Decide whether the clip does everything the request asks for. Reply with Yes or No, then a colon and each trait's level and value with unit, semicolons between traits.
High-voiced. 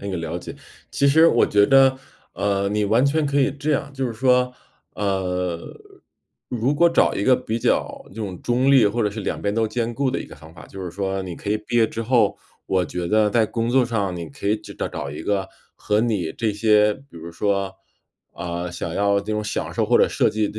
No: low, 105 Hz